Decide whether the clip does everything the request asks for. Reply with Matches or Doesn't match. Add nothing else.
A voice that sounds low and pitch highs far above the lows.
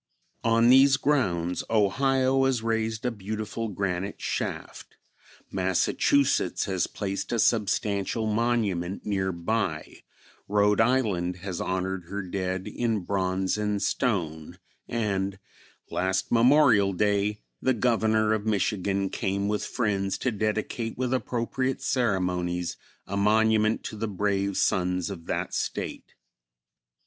Doesn't match